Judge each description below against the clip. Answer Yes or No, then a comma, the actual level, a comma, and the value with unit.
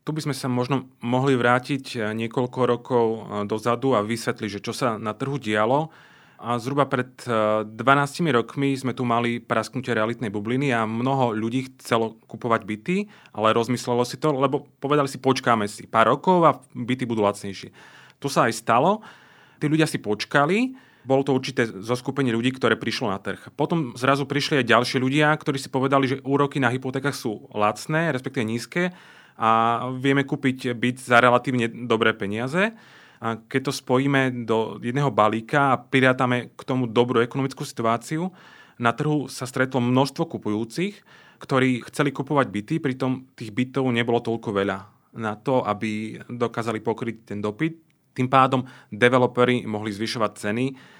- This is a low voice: Yes, low, 125 Hz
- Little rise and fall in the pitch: No, average, 3.2 semitones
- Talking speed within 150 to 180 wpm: Yes, average, 160 wpm